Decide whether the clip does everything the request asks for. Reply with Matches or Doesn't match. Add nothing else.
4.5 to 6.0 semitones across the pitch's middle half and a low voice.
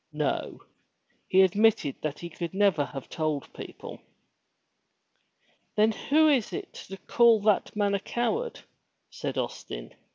Doesn't match